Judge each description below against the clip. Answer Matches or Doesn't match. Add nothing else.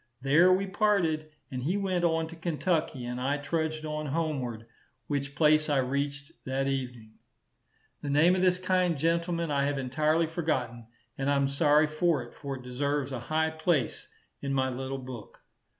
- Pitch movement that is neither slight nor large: Matches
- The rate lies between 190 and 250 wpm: Doesn't match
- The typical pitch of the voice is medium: Matches